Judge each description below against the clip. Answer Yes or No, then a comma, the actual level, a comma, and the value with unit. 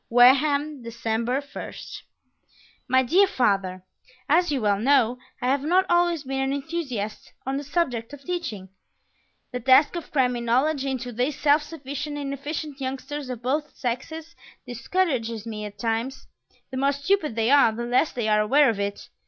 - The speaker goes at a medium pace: Yes, average, 160 wpm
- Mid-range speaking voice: No, very high, 265 Hz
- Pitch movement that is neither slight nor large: Yes, average, 4.1 semitones